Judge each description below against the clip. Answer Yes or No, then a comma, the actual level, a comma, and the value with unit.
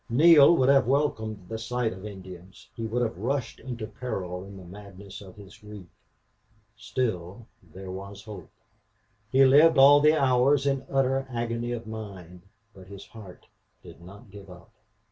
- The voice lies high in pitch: No, low, 110 Hz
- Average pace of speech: Yes, average, 165 wpm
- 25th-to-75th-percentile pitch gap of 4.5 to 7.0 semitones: Yes, average, 5.1 semitones